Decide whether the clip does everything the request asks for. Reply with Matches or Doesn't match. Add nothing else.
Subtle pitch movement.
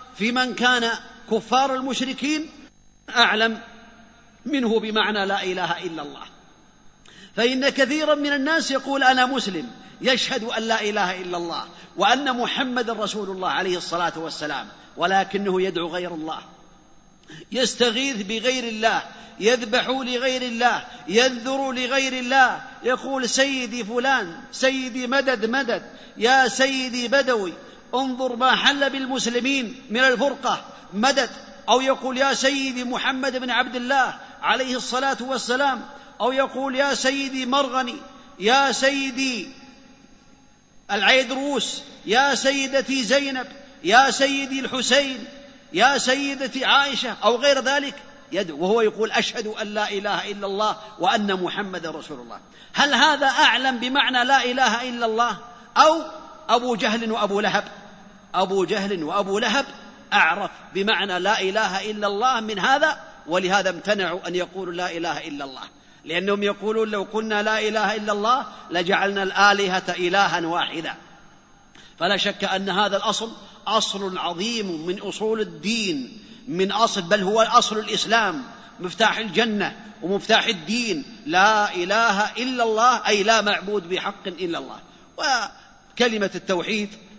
Doesn't match